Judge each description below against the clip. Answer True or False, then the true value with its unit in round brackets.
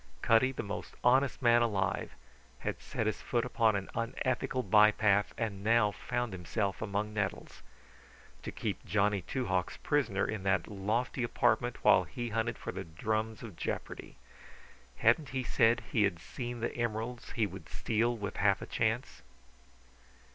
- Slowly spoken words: False (155 wpm)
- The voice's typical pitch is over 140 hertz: False (110 Hz)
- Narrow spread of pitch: False (3.0 semitones)